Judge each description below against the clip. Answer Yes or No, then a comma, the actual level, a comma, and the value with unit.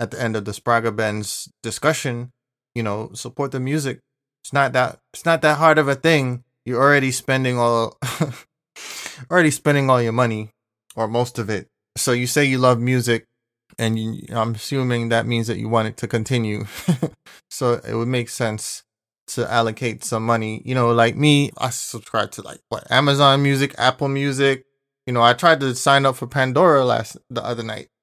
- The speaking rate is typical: Yes, average, 190 wpm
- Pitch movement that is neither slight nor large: Yes, average, 3.1 semitones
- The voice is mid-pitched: No, low, 125 Hz